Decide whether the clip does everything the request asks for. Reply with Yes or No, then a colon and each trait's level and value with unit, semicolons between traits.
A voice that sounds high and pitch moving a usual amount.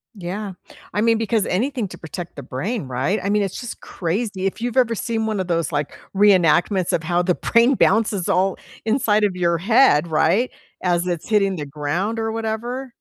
Yes: high, 195 Hz; average, 4.4 semitones